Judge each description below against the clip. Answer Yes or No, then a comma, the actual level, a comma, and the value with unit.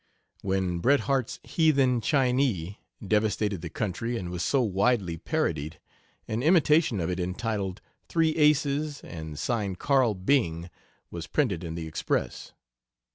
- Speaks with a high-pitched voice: No, low, 105 Hz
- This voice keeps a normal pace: No, slow, 130 wpm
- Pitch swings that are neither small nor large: No, wide, 7.6 semitones